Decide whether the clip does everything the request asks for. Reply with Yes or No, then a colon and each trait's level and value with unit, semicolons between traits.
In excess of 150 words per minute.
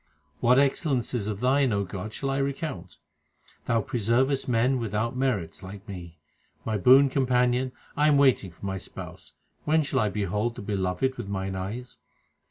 Yes: average, 165 wpm